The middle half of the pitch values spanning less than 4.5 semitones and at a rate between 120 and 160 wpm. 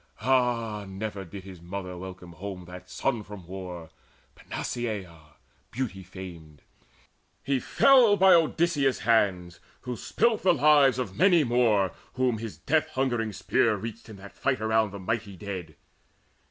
No: wide, 5.5 semitones; average, 140 wpm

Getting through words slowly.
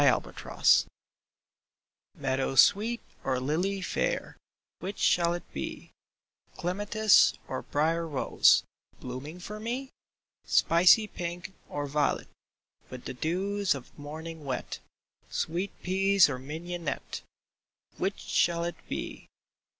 Yes: slow, 110 wpm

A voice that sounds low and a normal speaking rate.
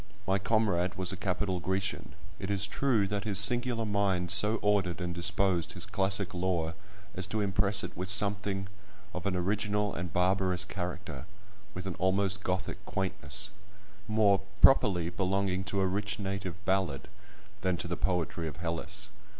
Yes: very low, 95 Hz; average, 155 wpm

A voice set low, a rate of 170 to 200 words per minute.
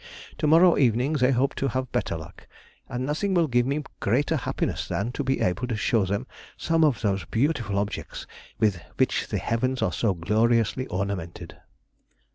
Yes: low, 120 Hz; average, 175 wpm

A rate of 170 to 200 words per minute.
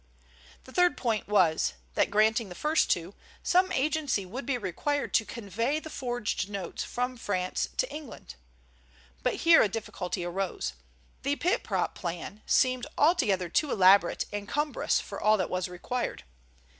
No: average, 155 wpm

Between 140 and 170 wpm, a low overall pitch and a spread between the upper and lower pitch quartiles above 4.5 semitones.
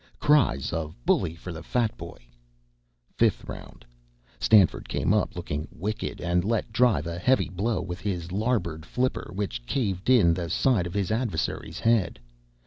Yes: average, 155 wpm; very low, 95 Hz; average, 5.2 semitones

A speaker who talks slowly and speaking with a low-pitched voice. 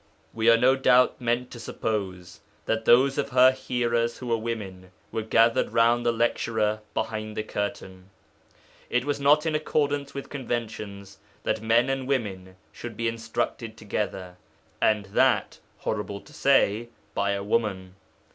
No: average, 150 wpm; low, 115 Hz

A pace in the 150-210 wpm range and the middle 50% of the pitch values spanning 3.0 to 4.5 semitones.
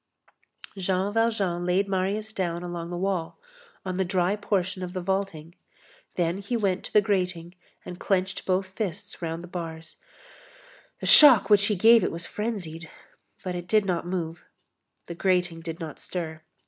No: average, 165 wpm; narrow, 2.5 semitones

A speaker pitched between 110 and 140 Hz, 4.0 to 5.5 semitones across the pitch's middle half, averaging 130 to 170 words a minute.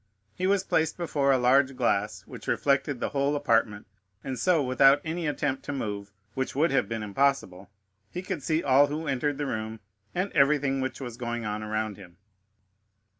No: low, 135 Hz; average, 4.3 semitones; average, 180 wpm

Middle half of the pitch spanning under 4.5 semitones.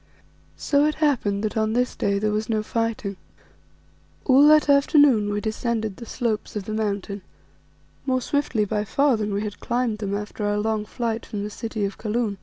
Yes: average, 2.8 semitones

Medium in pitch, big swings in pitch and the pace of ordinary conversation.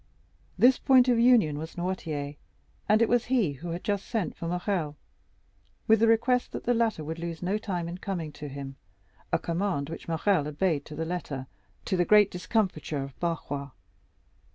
Yes: medium, 175 Hz; wide, 5.9 semitones; average, 175 wpm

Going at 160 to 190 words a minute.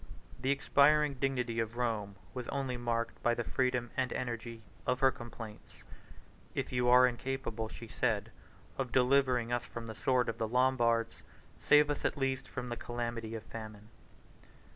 Yes: average, 165 wpm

